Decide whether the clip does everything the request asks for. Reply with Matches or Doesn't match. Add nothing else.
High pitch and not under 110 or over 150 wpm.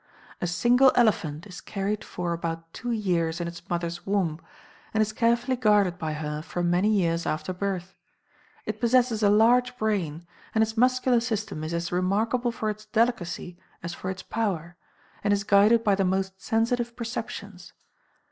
Doesn't match